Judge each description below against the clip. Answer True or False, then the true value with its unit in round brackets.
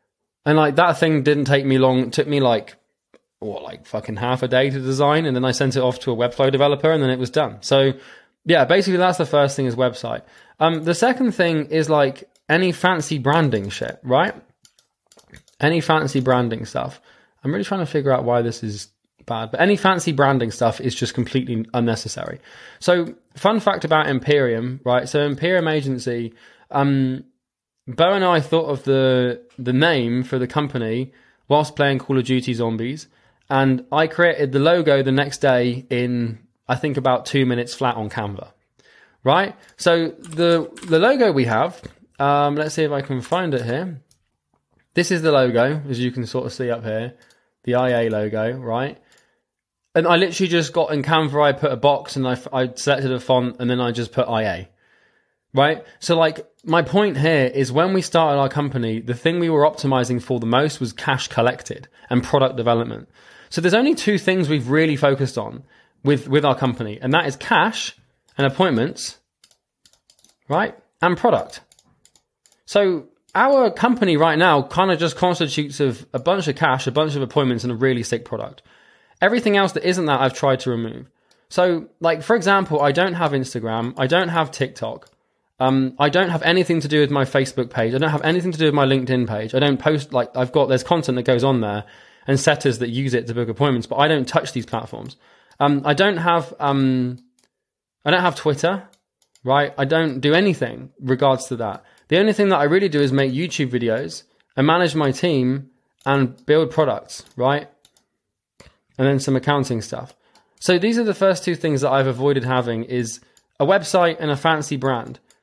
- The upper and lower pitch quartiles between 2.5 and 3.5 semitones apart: False (4.3 semitones)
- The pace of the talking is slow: False (195 wpm)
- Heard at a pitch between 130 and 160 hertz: True (140 Hz)